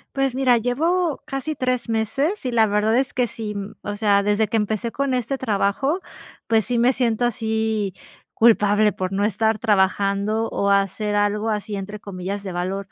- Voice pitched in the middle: No, high, 220 Hz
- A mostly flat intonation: No, average, 3.4 semitones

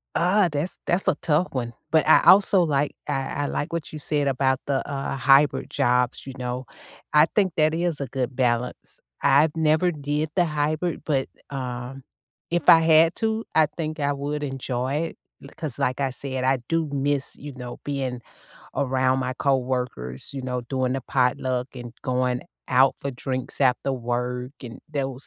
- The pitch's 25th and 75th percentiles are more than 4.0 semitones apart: No, average, 3.1 semitones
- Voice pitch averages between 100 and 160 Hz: Yes, low, 135 Hz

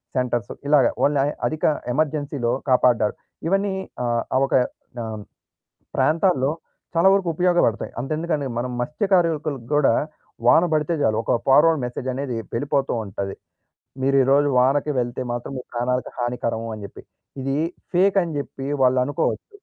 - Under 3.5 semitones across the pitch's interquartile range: No, average, 4.1 semitones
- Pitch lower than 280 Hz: Yes, low, 135 Hz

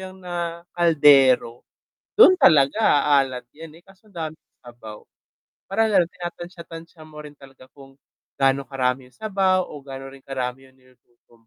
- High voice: No, medium, 145 Hz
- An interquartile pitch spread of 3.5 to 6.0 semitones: Yes, average, 4.7 semitones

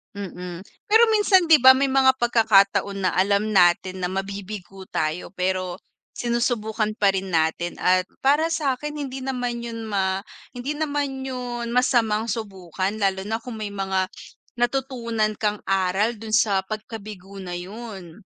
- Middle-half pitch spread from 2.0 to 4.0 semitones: No, average, 4.5 semitones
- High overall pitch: Yes, high, 215 Hz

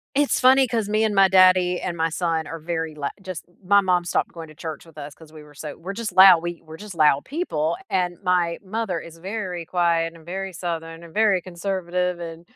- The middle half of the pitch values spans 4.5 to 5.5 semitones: No, average, 2.7 semitones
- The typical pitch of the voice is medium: Yes, medium, 175 Hz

